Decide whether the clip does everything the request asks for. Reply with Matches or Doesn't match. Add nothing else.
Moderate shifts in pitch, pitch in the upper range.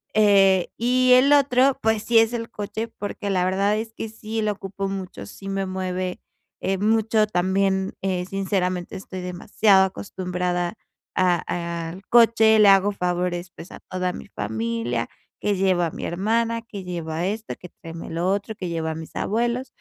Matches